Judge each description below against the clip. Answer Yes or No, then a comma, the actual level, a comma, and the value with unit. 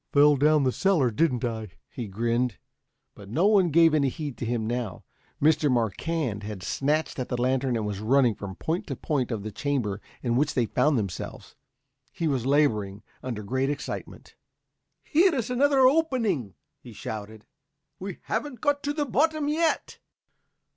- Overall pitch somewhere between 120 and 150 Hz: Yes, low, 135 Hz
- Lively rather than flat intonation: Yes, wide, 6.9 semitones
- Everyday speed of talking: Yes, average, 165 wpm